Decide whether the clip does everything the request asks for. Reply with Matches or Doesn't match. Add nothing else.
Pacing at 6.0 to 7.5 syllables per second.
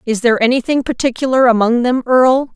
Matches